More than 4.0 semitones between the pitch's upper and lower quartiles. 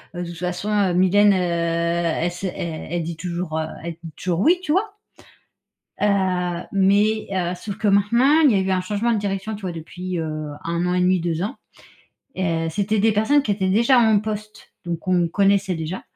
No: average, 3.3 semitones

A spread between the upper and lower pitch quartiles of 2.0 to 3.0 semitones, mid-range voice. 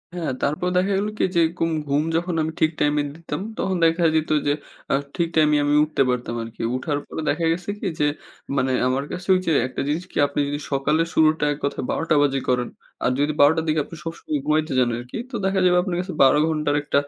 Yes: average, 2.7 semitones; medium, 155 Hz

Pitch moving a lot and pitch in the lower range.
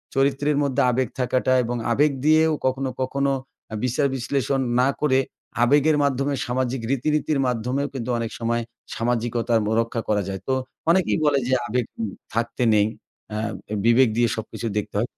No: average, 3.0 semitones; low, 130 Hz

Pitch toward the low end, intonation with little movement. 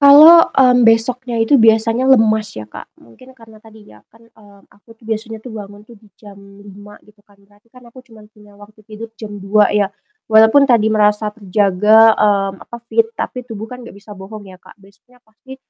No: high, 220 Hz; narrow, 2.1 semitones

